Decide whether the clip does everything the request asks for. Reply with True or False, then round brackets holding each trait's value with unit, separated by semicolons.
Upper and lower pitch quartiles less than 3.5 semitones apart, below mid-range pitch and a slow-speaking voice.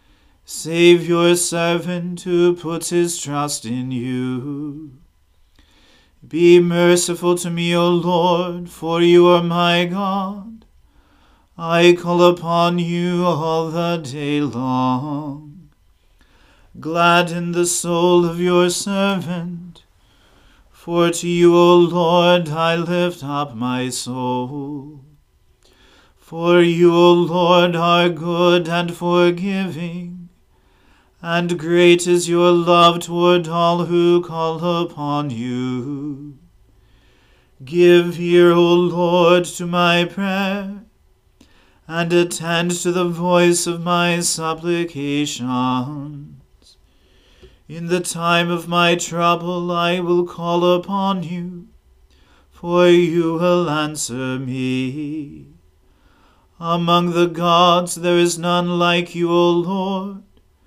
False (3.0 semitones; 170 Hz; 105 wpm)